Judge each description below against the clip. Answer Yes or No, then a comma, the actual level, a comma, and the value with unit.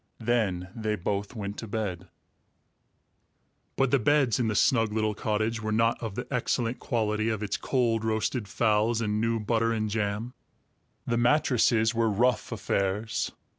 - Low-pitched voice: Yes, low, 110 Hz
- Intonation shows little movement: Yes, narrow, 1.9 semitones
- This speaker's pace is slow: No, average, 155 wpm